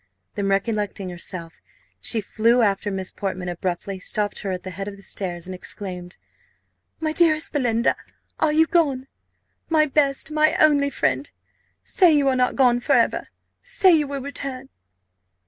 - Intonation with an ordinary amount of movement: No, wide, 7.0 semitones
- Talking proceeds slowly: No, average, 160 wpm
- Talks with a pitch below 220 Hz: No, high, 235 Hz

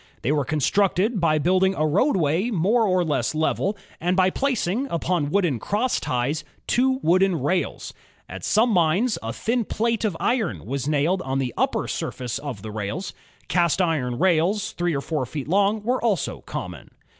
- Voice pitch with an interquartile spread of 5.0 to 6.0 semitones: Yes, wide, 5.6 semitones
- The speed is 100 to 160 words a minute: No, average, 170 wpm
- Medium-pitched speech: Yes, medium, 180 Hz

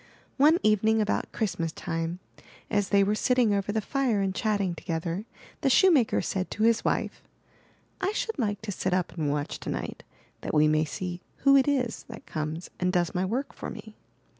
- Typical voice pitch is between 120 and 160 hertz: No, high, 205 Hz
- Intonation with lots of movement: No, average, 5.0 semitones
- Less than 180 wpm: No, average, 190 wpm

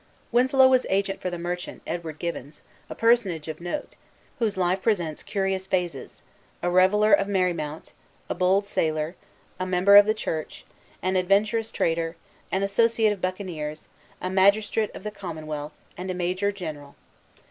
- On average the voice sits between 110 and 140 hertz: No, medium, 185 Hz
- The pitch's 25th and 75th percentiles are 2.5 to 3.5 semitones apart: Yes, average, 3.2 semitones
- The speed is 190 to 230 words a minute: No, average, 160 wpm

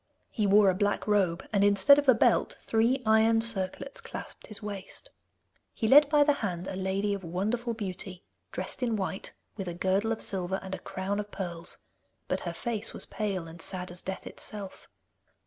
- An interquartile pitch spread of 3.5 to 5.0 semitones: No, average, 2.9 semitones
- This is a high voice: Yes, high, 200 Hz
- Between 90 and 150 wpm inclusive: No, average, 190 wpm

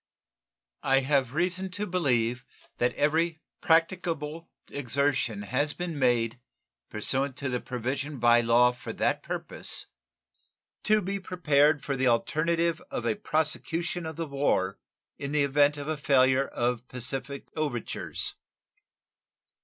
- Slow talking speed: Yes, slow, 130 wpm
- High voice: No, medium, 140 Hz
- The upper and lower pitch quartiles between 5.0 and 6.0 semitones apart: No, average, 4.4 semitones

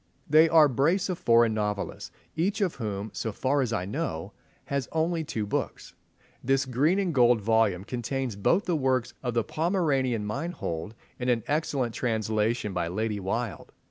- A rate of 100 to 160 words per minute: No, average, 170 wpm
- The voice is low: Yes, low, 125 Hz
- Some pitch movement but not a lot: No, wide, 5.7 semitones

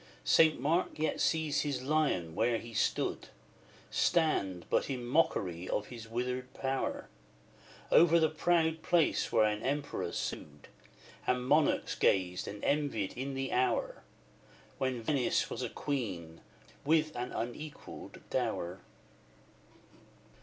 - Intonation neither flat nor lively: No, wide, 6.2 semitones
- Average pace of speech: No, slow, 125 wpm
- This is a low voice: Yes, low, 130 Hz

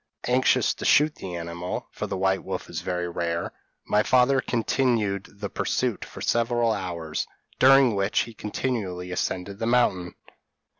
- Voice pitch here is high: No, low, 100 Hz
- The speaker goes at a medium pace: Yes, average, 155 wpm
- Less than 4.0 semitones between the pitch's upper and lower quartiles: No, average, 5.1 semitones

